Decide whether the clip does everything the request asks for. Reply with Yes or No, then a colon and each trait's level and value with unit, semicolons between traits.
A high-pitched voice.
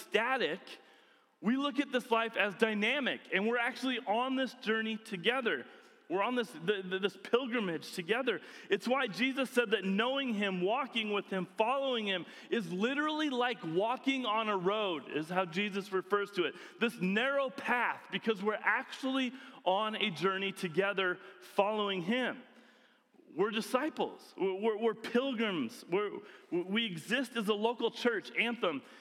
Yes: high, 230 Hz